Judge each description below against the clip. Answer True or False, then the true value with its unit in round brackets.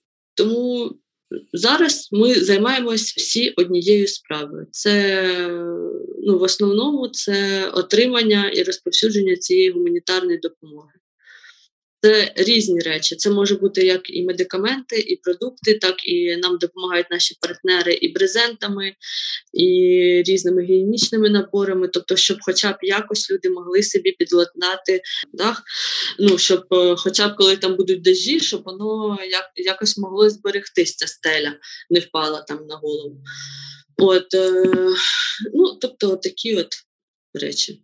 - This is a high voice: True (200 Hz)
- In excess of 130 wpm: False (120 wpm)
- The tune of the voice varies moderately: False (5.7 semitones)